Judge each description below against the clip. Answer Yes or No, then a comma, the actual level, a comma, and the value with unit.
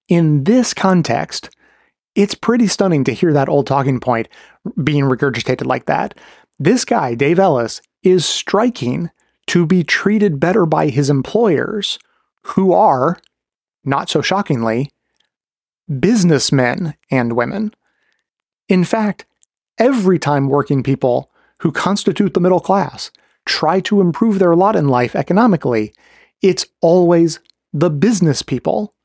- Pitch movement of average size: No, wide, 6.5 semitones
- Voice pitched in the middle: Yes, medium, 170 Hz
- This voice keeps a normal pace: No, slow, 125 wpm